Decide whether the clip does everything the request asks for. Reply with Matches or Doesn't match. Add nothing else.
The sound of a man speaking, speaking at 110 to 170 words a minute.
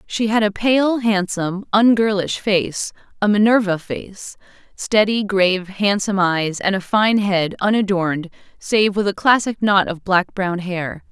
Doesn't match